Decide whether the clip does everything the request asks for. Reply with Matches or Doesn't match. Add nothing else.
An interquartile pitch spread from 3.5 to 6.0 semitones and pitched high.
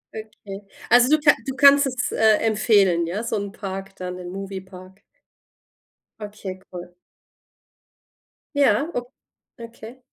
Matches